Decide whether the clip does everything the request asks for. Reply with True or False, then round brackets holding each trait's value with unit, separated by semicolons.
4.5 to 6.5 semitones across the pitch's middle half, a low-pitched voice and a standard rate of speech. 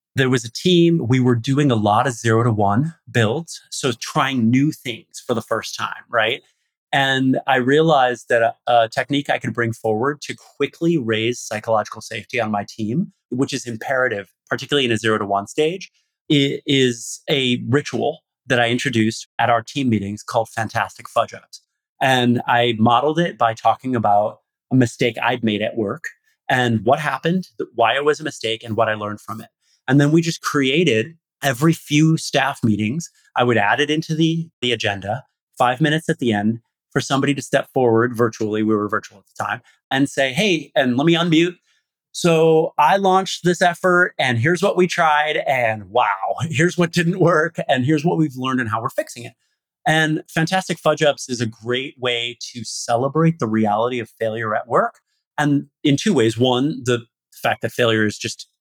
True (5.0 semitones; 130 Hz; 190 wpm)